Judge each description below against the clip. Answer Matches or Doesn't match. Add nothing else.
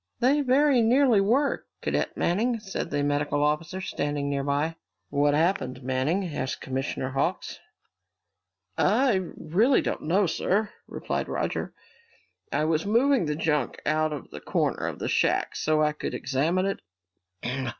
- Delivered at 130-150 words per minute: Matches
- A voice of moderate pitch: Matches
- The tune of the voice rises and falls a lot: Matches